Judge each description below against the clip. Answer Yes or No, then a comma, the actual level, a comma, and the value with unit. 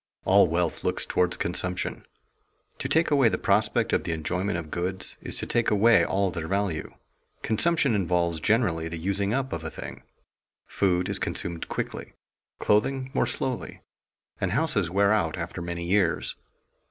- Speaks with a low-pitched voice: Yes, very low, 95 Hz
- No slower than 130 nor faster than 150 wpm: No, average, 165 wpm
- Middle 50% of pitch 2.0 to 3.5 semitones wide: No, average, 4.0 semitones